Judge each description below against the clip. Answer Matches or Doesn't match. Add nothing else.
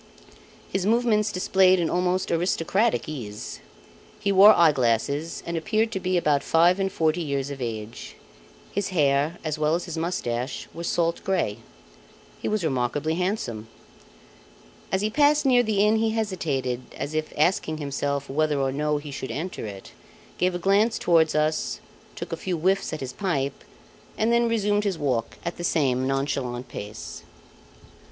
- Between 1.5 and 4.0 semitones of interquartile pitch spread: Doesn't match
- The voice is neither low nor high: Matches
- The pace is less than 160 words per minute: Doesn't match